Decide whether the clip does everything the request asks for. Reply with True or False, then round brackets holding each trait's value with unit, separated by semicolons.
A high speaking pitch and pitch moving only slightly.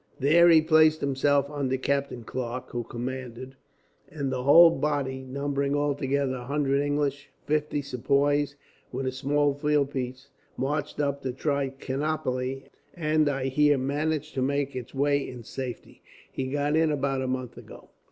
False (140 Hz; 1.9 semitones)